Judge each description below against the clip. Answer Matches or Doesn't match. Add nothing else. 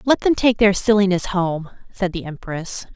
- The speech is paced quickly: Doesn't match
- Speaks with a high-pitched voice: Matches